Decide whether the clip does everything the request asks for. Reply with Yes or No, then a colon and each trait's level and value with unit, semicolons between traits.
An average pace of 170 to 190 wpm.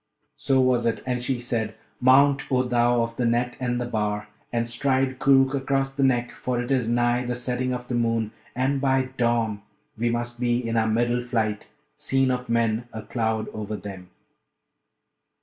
Yes: average, 185 wpm